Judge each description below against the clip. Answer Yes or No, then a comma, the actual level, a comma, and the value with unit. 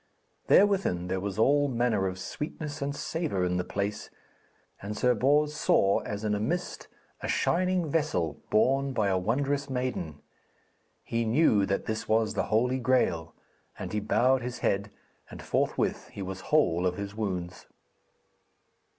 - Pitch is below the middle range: Yes, low, 110 Hz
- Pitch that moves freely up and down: Yes, wide, 6.2 semitones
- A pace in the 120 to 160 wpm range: Yes, average, 155 wpm